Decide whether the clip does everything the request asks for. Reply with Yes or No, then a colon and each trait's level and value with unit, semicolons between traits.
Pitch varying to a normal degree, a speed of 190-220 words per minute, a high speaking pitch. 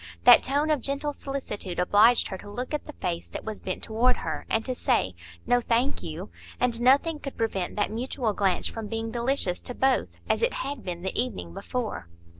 Yes: average, 4.7 semitones; fast, 205 wpm; high, 235 Hz